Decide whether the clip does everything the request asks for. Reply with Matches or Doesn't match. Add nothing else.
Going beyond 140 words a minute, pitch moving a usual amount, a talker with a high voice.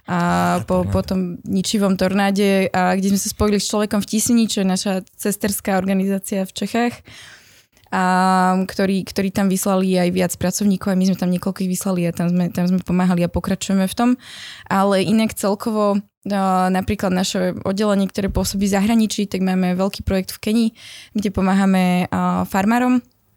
Doesn't match